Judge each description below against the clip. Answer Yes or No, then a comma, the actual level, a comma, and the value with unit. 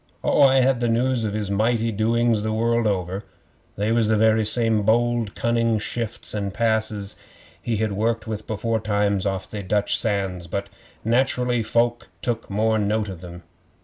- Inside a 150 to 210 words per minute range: Yes, average, 165 wpm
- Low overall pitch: Yes, low, 110 Hz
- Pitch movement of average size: No, narrow, 2.3 semitones